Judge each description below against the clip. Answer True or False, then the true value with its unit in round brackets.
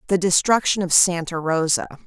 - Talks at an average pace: True (145 wpm)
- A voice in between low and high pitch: True (175 Hz)